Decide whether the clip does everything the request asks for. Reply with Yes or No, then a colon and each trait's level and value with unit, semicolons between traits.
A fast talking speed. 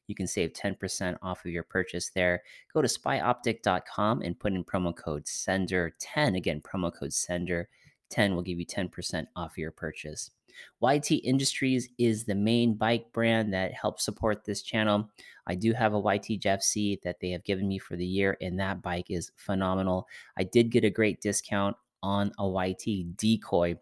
No: average, 180 wpm